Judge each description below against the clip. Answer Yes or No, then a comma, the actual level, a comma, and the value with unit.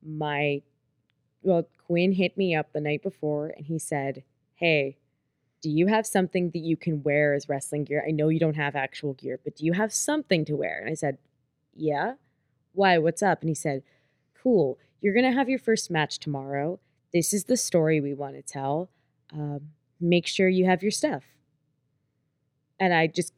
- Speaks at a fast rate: No, average, 195 wpm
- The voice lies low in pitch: No, medium, 150 Hz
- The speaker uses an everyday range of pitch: Yes, average, 3.6 semitones